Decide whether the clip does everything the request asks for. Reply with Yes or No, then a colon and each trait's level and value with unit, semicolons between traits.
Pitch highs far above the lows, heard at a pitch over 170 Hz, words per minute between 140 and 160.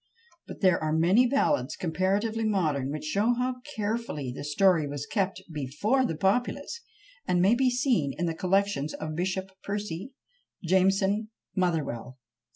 Yes: wide, 5.7 semitones; high, 190 Hz; average, 150 wpm